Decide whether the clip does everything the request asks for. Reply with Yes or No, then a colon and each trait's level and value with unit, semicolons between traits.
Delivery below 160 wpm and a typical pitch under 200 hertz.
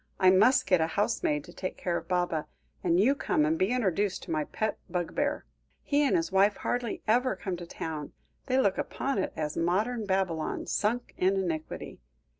No: average, 190 wpm; high, 190 Hz